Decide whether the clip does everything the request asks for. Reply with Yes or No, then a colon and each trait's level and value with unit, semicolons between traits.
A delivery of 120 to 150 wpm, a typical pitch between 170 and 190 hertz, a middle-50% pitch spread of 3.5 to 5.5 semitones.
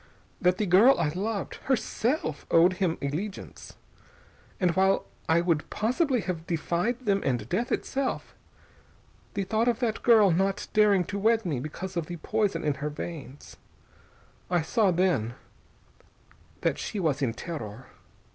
Yes: average, 145 wpm; medium, 185 Hz; average, 5.0 semitones